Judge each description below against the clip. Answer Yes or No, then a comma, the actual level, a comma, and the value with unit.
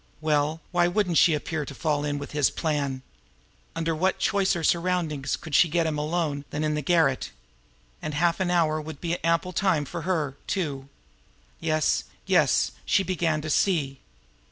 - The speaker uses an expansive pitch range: No, average, 2.8 semitones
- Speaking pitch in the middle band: Yes, medium, 160 Hz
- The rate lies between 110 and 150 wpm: No, average, 170 wpm